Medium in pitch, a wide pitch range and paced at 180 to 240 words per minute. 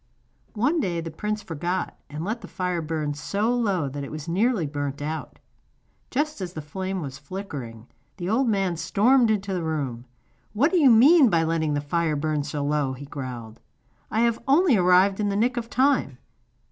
Yes: medium, 180 Hz; wide, 6.9 semitones; average, 190 wpm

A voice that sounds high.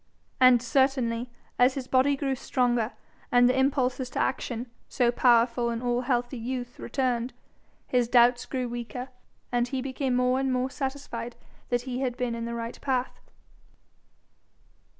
Yes: very high, 250 Hz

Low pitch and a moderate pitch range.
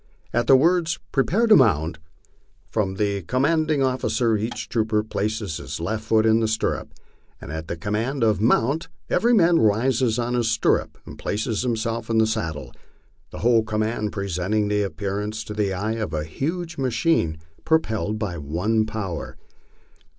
Yes: low, 110 Hz; average, 3.6 semitones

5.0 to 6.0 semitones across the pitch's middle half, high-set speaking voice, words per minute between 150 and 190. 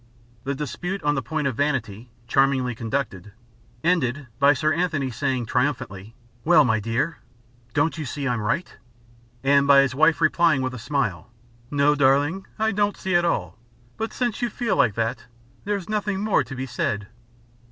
No: average, 5.3 semitones; medium, 140 Hz; average, 170 wpm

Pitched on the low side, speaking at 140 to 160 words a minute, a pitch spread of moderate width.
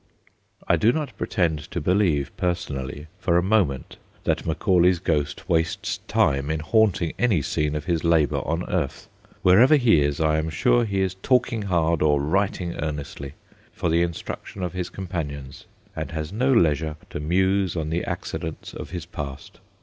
No: very low, 85 Hz; average, 170 wpm; average, 3.8 semitones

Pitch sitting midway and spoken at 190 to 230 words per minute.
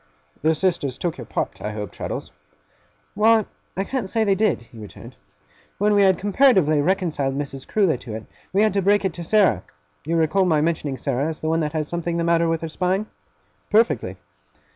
Yes: medium, 170 Hz; average, 200 wpm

